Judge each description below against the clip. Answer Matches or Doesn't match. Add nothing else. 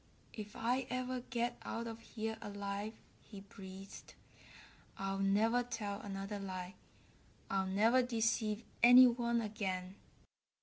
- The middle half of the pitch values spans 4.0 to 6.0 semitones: Doesn't match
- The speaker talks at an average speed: Doesn't match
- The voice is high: Matches